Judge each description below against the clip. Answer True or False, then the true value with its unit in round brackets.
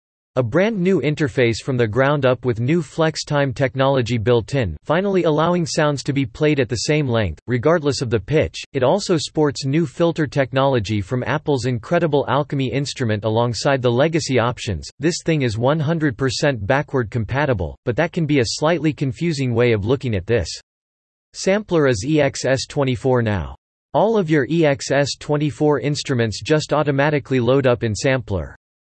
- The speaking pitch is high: False (135 Hz)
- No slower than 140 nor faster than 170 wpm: True (160 wpm)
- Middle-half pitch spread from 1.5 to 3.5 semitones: False (3.9 semitones)